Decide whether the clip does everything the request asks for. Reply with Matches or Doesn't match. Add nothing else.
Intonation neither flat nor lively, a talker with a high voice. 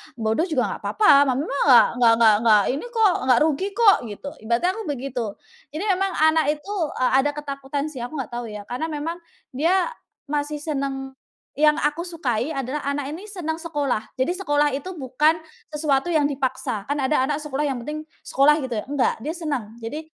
Matches